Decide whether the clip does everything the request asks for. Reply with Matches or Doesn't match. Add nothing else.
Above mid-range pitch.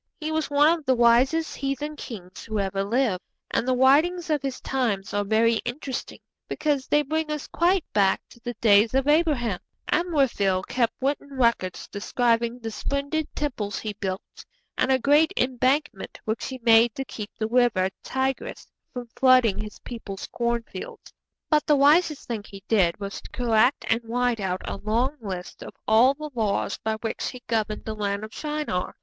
Matches